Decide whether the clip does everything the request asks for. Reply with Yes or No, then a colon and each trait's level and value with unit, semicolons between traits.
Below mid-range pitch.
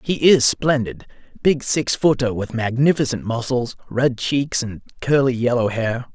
Yes: low, 125 Hz